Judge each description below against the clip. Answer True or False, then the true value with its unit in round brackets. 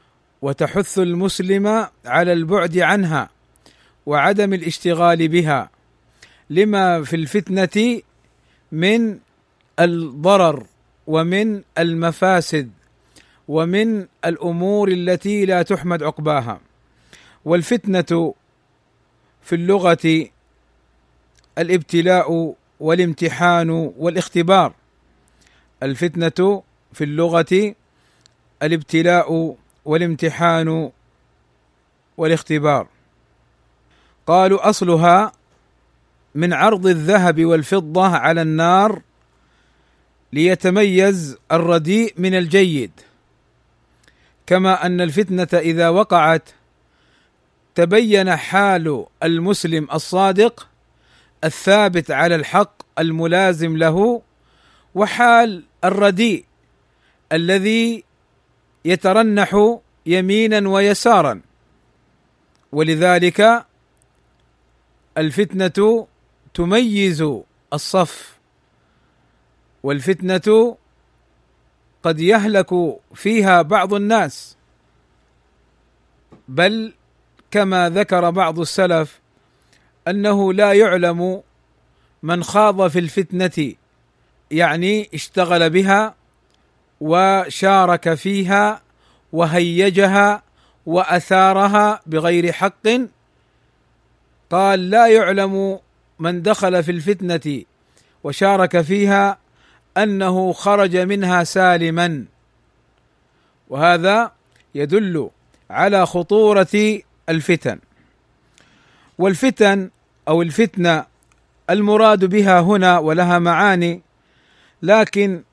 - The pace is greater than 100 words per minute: False (65 wpm)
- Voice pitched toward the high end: False (180 Hz)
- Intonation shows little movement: False (3.4 semitones)